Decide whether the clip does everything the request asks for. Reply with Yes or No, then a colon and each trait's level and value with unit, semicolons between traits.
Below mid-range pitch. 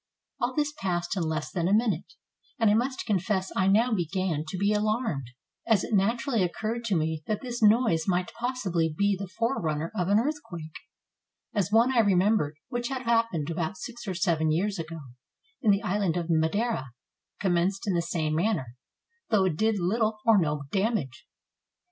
No: high, 195 Hz